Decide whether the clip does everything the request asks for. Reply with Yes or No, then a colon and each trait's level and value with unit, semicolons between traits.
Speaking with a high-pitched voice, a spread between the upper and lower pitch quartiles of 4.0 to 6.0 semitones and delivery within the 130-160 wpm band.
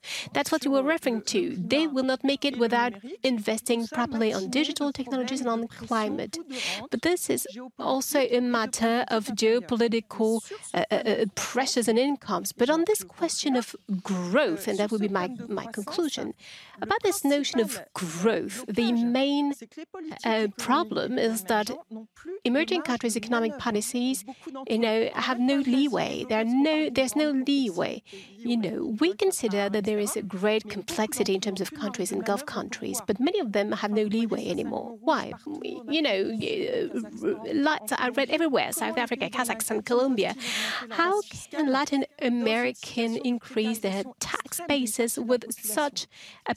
Yes: high, 245 Hz; average, 4.3 semitones; average, 155 wpm